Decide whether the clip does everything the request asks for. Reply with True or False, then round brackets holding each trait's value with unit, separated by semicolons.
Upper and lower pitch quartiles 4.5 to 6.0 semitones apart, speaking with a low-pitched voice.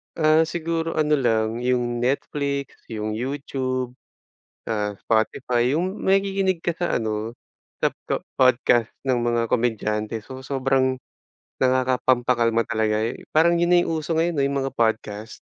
True (5.1 semitones; 130 Hz)